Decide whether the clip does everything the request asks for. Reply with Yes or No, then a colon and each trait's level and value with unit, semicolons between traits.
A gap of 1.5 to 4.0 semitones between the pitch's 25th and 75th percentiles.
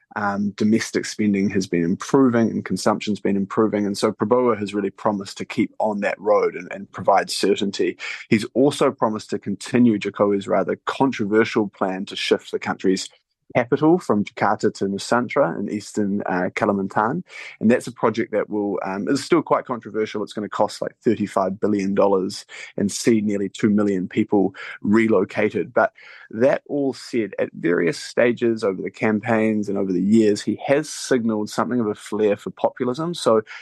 Yes: average, 3.0 semitones